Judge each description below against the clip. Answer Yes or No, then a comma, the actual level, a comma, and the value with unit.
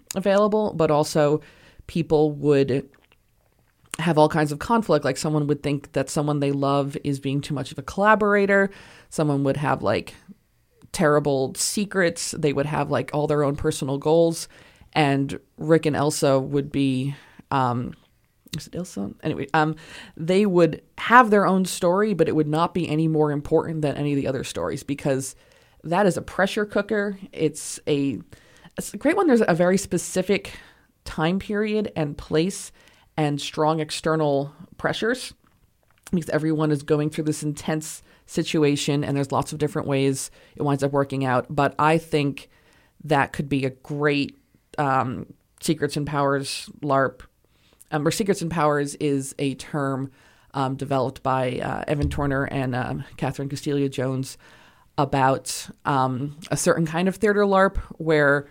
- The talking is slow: No, average, 160 wpm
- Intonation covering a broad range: No, average, 3.0 semitones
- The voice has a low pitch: No, medium, 150 Hz